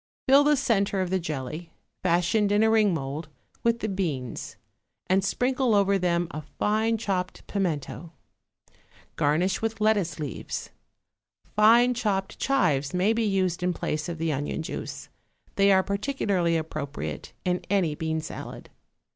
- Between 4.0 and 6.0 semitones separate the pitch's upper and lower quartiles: Yes, average, 4.7 semitones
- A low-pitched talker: No, medium, 185 Hz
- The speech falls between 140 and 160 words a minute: Yes, average, 145 wpm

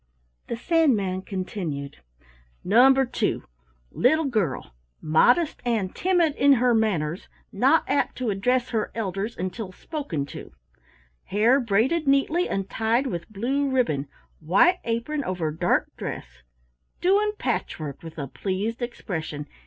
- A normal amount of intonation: No, wide, 6.5 semitones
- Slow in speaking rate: Yes, slow, 125 wpm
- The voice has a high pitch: Yes, high, 225 Hz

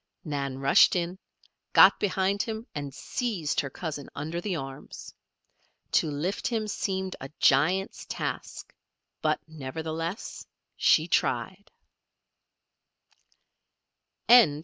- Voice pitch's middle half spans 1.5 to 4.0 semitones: No, average, 4.9 semitones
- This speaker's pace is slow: Yes, slow, 100 wpm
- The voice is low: No, medium, 165 Hz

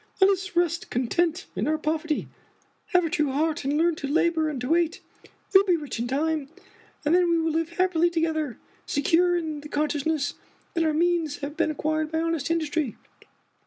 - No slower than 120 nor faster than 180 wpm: No, average, 200 wpm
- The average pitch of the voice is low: No, very high, 320 Hz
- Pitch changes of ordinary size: No, narrow, 2.2 semitones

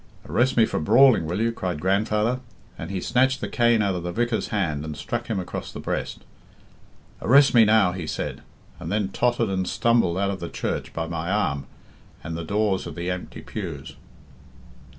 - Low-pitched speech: Yes, low, 100 Hz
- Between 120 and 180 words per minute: No, average, 190 wpm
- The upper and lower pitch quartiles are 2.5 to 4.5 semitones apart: No, average, 4.9 semitones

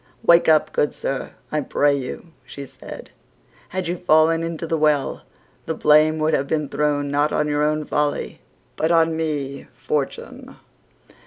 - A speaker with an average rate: Yes, average, 160 wpm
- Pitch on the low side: No, medium, 150 Hz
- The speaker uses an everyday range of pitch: No, narrow, 1.9 semitones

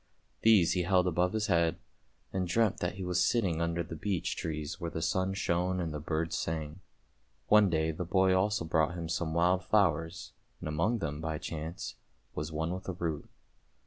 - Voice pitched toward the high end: No, very low, 85 Hz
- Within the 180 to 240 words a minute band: Yes, average, 190 wpm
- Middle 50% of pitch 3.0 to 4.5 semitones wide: No, narrow, 2.5 semitones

